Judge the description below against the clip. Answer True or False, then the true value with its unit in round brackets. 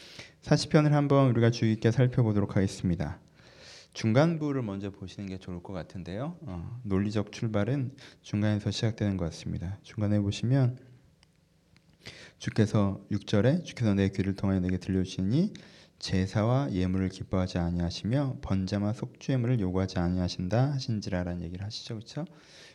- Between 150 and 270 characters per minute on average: False (345 characters per minute)